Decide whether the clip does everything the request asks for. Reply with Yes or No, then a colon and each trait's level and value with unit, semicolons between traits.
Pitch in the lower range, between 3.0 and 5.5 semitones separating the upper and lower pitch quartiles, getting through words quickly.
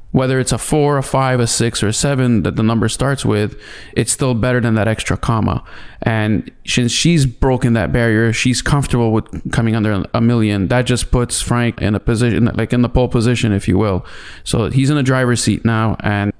No: low, 120 Hz; narrow, 2.5 semitones; fast, 215 wpm